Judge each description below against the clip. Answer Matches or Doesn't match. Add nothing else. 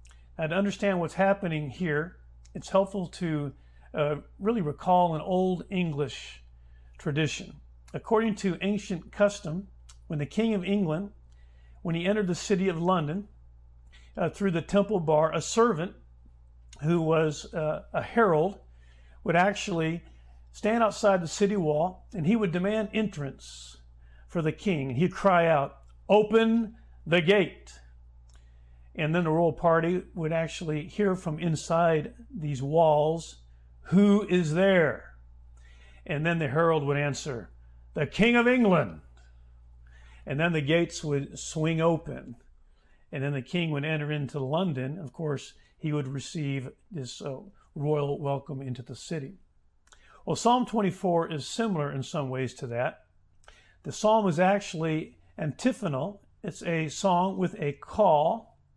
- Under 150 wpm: Matches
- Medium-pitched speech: Matches